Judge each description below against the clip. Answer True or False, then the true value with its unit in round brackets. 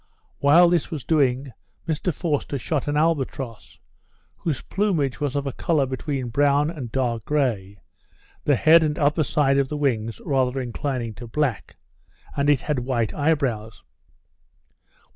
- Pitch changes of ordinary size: True (3.3 semitones)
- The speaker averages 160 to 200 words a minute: False (150 wpm)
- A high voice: False (140 Hz)